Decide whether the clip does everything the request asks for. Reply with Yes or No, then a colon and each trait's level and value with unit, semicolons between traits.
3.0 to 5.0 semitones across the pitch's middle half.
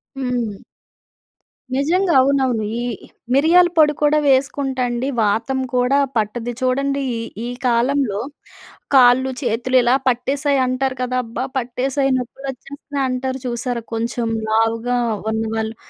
No: narrow, 2.5 semitones